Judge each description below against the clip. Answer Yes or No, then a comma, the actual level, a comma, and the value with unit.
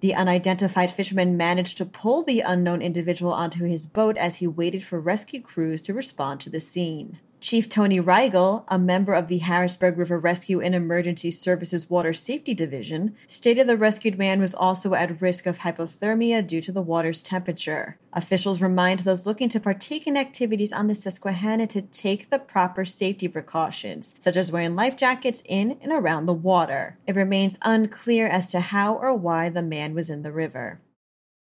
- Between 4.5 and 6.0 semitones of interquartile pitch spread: No, average, 3.3 semitones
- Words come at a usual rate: Yes, average, 180 wpm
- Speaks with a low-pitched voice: No, medium, 185 Hz